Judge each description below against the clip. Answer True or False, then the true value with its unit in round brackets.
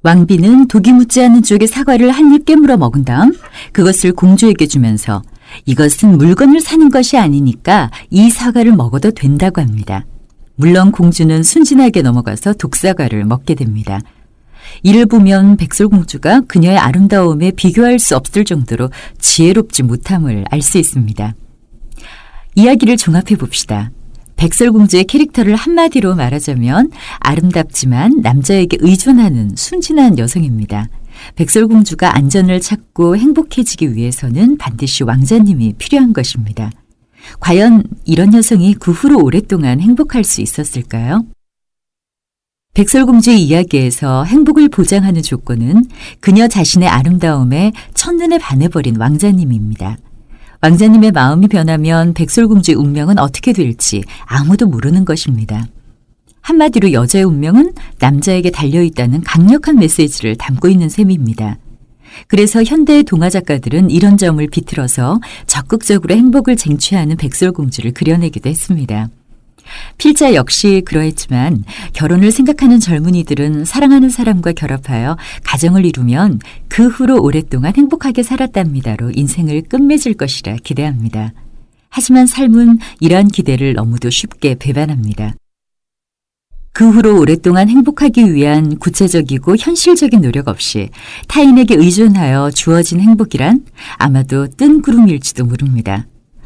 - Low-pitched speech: False (175 Hz)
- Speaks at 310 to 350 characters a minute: True (325 characters per minute)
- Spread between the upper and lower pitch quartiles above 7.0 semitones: True (8.8 semitones)